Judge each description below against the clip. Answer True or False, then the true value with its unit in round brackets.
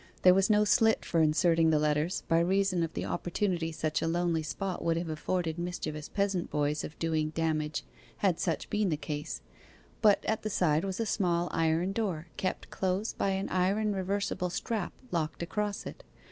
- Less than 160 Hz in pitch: False (175 Hz)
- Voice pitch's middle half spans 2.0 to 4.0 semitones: True (3.5 semitones)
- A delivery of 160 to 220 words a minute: True (185 wpm)